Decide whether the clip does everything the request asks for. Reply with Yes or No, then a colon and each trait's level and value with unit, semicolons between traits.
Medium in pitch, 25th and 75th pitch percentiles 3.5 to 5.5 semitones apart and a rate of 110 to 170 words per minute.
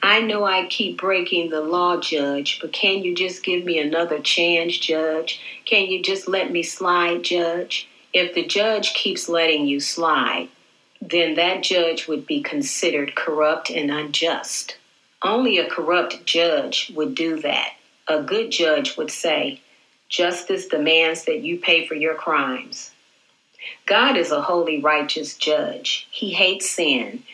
No: medium, 170 Hz; average, 3.1 semitones; average, 150 wpm